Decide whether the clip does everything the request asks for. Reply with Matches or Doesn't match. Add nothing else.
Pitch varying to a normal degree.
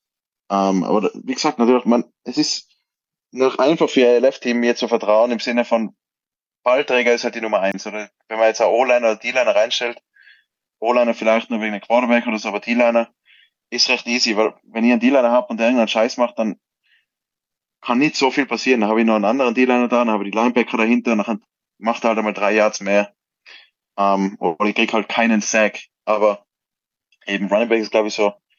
Doesn't match